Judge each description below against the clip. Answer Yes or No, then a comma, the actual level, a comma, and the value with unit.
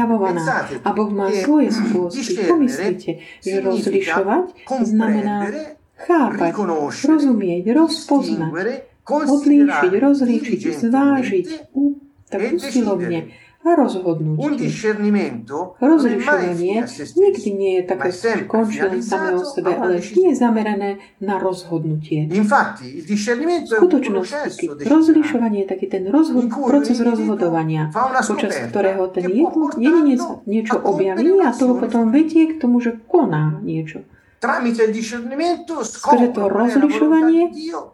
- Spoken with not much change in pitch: No, wide, 7.0 semitones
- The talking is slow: Yes, slow, 100 wpm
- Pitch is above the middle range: Yes, high, 235 Hz